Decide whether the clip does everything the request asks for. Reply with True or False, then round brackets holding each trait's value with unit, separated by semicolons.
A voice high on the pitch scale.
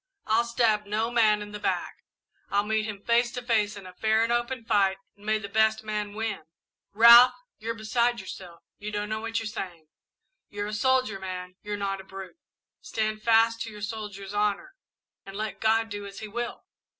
True (215 Hz)